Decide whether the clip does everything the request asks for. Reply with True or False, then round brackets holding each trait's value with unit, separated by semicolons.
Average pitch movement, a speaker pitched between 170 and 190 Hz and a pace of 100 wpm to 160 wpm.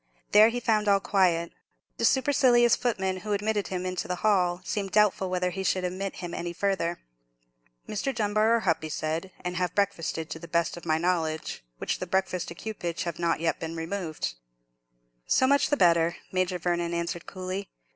False (3.2 semitones; 185 Hz; 185 wpm)